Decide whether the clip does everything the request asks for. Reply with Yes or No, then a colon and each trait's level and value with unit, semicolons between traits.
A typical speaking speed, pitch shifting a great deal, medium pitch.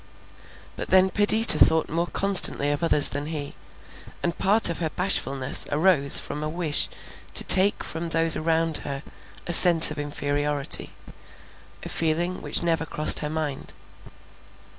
No: average, 145 wpm; average, 2.9 semitones; medium, 160 Hz